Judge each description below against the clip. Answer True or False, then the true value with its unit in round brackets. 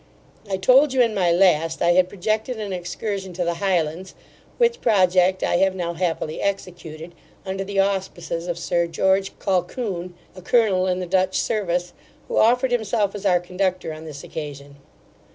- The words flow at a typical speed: True (170 wpm)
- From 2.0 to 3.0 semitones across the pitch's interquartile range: True (2.4 semitones)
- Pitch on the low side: False (185 Hz)